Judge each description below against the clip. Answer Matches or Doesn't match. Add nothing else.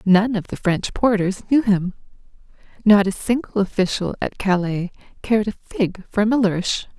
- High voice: Matches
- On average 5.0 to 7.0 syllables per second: Doesn't match